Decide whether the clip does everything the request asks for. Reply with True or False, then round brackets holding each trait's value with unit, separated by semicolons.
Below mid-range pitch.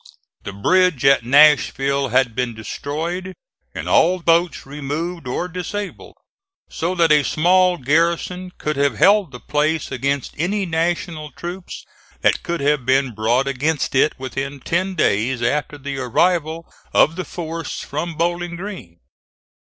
False (155 Hz)